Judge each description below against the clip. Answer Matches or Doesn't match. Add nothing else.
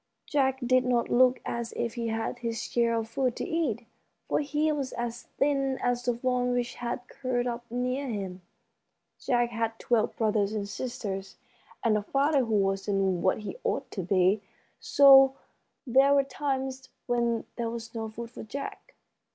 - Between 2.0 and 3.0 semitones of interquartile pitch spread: Matches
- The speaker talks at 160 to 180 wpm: Matches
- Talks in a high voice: Matches